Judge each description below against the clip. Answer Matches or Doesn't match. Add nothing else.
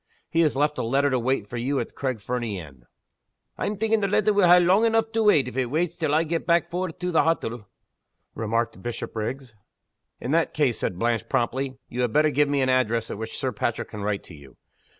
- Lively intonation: Matches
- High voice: Doesn't match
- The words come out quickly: Matches